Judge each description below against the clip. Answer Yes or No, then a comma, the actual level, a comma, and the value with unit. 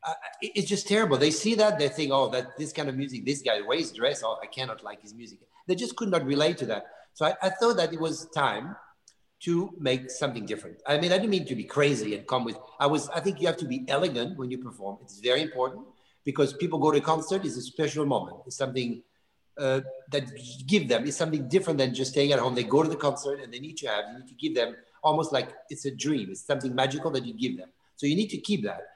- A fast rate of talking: Yes, fast, 265 wpm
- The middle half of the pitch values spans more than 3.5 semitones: Yes, average, 3.9 semitones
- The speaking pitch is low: No, medium, 145 Hz